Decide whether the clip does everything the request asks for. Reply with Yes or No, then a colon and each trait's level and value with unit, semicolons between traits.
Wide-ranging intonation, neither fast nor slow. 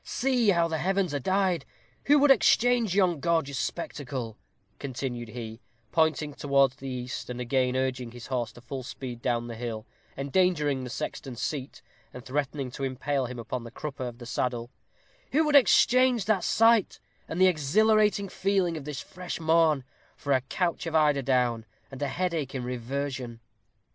Yes: wide, 6.1 semitones; average, 170 wpm